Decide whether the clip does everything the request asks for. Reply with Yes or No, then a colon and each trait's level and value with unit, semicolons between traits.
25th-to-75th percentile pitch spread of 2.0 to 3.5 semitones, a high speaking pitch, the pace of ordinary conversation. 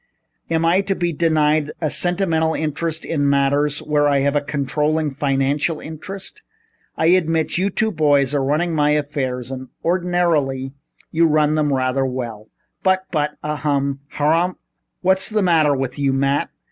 No: average, 3.0 semitones; medium, 150 Hz; average, 160 wpm